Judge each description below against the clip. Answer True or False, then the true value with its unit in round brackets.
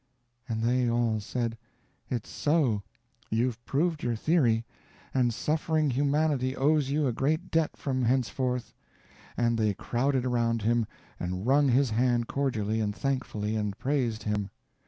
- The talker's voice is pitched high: False (125 Hz)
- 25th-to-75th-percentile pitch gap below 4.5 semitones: True (3.6 semitones)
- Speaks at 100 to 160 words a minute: True (140 wpm)